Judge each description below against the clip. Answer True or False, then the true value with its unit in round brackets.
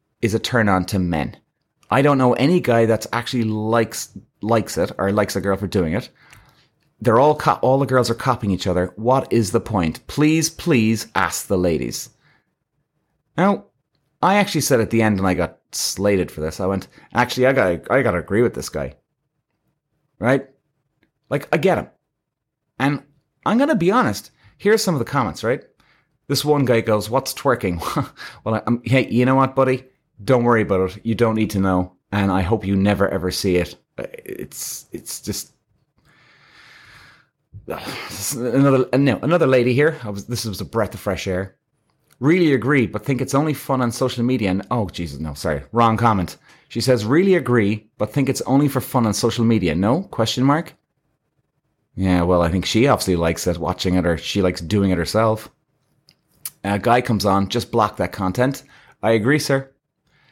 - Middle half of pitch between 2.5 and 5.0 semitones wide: False (5.6 semitones)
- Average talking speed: True (190 wpm)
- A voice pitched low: True (115 Hz)